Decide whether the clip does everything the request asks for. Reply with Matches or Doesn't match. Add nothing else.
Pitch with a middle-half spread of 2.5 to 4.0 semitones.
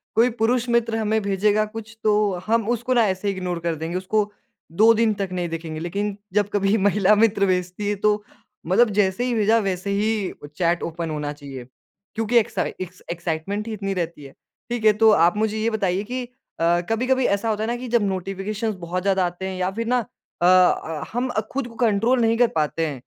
Matches